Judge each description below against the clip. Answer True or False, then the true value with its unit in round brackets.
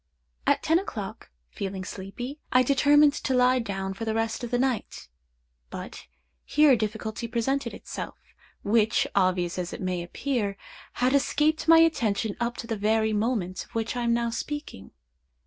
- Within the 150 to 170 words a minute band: True (165 wpm)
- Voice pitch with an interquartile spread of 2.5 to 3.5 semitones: False (4.5 semitones)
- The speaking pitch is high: True (230 Hz)